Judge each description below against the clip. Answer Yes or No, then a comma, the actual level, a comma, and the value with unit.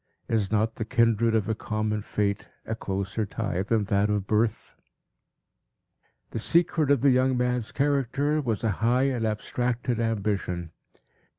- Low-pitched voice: Yes, low, 110 Hz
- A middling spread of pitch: Yes, average, 3.0 semitones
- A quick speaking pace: No, average, 150 wpm